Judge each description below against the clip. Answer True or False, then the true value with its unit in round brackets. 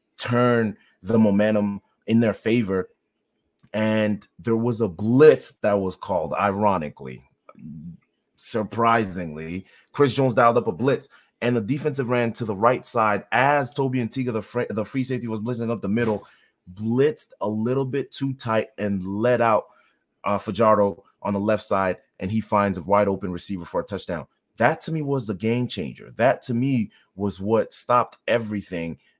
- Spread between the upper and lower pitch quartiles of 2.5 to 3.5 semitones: True (3.1 semitones)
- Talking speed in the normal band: True (165 wpm)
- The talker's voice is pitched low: True (110 Hz)